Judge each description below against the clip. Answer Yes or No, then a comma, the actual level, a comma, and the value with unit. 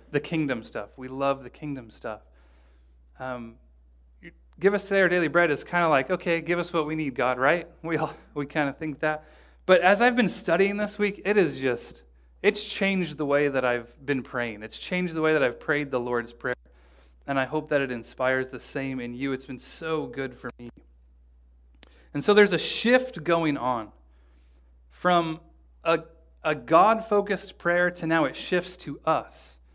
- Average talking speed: Yes, average, 190 wpm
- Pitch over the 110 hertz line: Yes, medium, 140 Hz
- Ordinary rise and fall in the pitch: No, wide, 7.6 semitones